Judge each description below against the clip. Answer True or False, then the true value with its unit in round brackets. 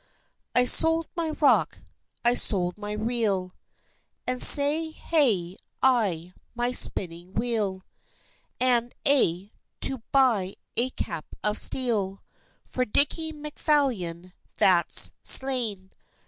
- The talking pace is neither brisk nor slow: False (105 wpm)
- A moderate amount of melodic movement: False (6.0 semitones)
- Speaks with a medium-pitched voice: False (235 Hz)